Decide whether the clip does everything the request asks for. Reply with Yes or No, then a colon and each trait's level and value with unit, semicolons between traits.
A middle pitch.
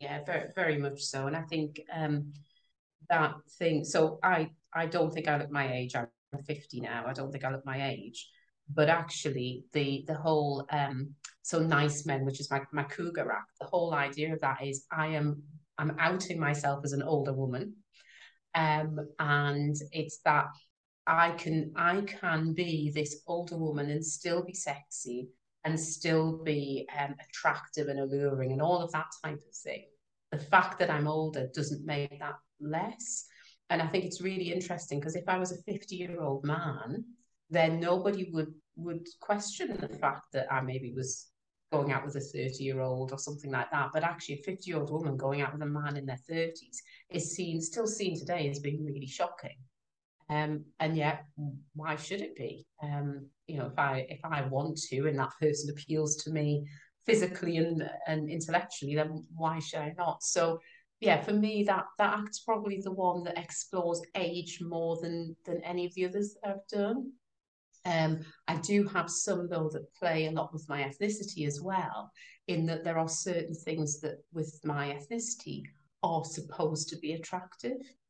Yes: medium, 155 Hz